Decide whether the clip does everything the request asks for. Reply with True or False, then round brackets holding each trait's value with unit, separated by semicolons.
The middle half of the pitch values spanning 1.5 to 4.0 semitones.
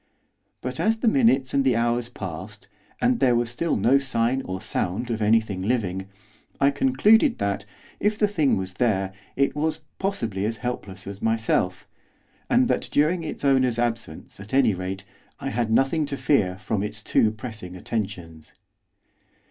False (5.6 semitones)